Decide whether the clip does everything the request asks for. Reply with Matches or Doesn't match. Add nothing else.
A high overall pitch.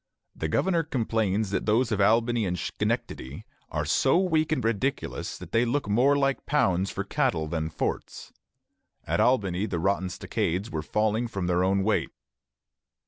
Doesn't match